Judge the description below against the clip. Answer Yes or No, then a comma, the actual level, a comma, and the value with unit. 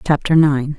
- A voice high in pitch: No, medium, 145 Hz